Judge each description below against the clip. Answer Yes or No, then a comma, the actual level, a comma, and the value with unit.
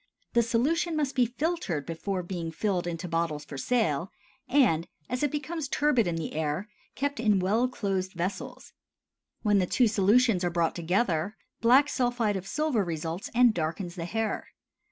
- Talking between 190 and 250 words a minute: No, average, 165 wpm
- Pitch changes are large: Yes, wide, 6.5 semitones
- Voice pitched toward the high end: Yes, high, 200 Hz